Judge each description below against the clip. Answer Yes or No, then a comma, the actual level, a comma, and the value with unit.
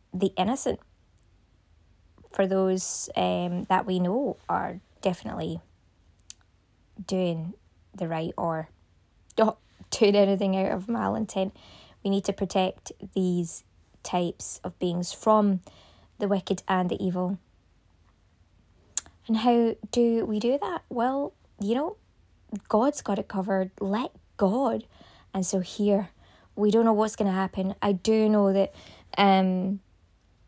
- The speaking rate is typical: No, slow, 130 wpm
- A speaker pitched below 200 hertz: Yes, high, 190 Hz